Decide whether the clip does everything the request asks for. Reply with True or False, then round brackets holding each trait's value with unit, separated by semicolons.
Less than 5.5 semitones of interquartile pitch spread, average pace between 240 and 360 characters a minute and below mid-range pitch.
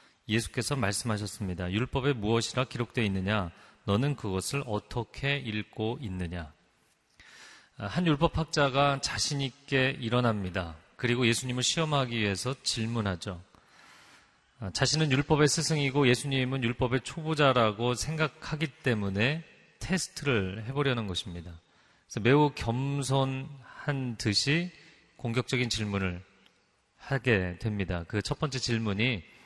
True (5.1 semitones; 285 characters per minute; 120 Hz)